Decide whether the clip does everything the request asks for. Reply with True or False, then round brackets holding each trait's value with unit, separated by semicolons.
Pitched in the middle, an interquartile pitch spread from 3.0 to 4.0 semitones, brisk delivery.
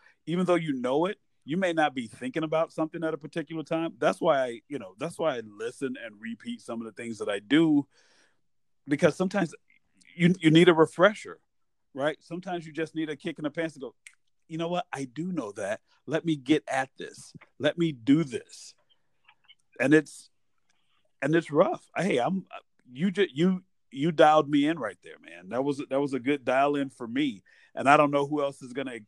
True (160 Hz; 3.7 semitones; 215 wpm)